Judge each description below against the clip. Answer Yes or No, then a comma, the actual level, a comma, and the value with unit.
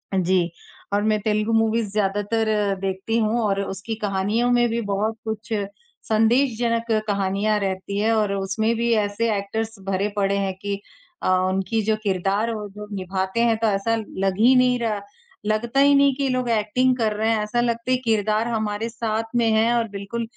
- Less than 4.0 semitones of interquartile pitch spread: Yes, narrow, 2.5 semitones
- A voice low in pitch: No, high, 215 Hz